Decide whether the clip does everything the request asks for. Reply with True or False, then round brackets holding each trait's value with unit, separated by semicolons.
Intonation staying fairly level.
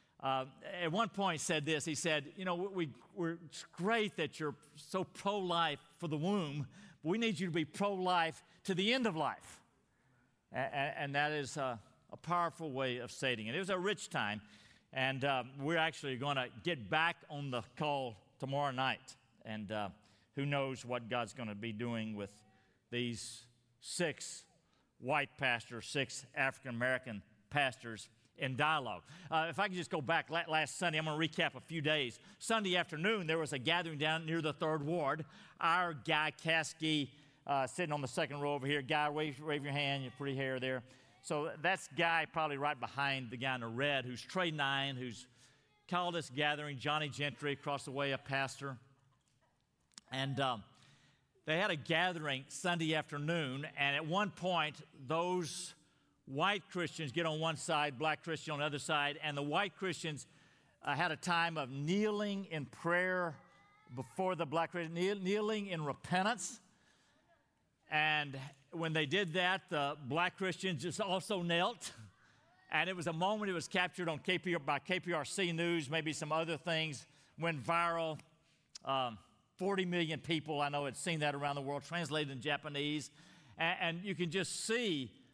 False (3.9 semitones)